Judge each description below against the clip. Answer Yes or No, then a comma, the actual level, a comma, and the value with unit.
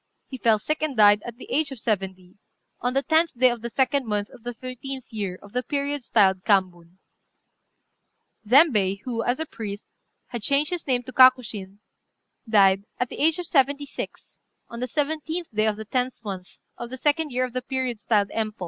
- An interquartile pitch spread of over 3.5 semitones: Yes, average, 4.7 semitones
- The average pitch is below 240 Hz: No, high, 245 Hz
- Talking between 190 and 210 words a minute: Yes, average, 200 wpm